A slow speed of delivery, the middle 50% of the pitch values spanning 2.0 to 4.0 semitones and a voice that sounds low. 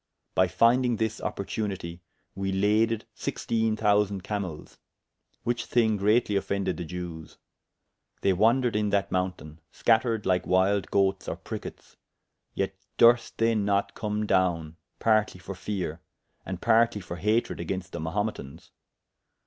Yes: slow, 130 wpm; average, 3.2 semitones; low, 100 Hz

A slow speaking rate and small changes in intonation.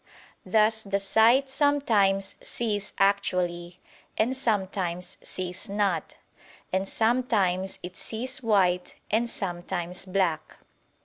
No: slow, 100 wpm; average, 3.5 semitones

